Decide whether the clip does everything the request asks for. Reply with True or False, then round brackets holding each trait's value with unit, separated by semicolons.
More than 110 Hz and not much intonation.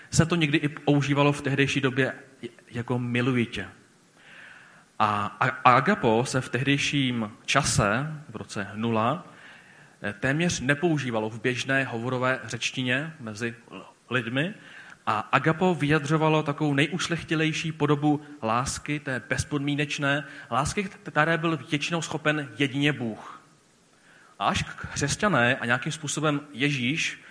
False (140 Hz; 3.6 semitones)